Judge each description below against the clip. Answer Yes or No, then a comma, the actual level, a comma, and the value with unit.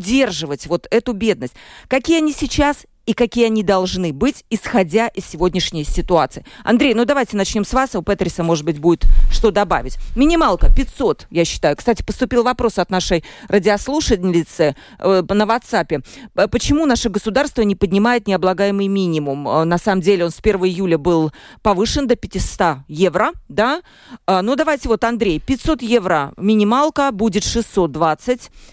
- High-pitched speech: Yes, high, 205 Hz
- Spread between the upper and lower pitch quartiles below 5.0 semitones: No, wide, 5.4 semitones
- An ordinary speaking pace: Yes, average, 150 wpm